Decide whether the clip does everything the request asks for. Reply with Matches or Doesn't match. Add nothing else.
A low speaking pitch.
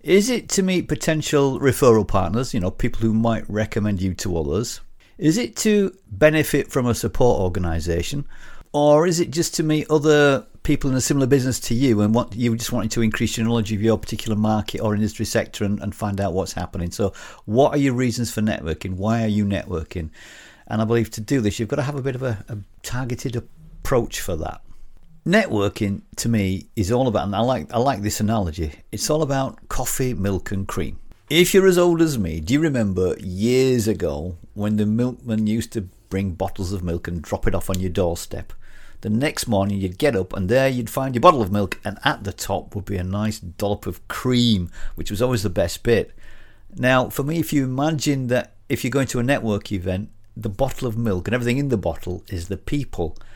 Matches